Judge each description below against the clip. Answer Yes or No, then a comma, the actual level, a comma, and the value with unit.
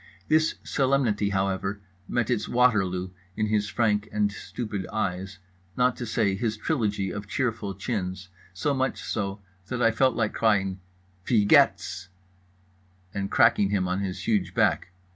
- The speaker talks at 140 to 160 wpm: Yes, average, 145 wpm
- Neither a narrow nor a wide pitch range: Yes, average, 3.0 semitones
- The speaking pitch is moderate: No, low, 105 Hz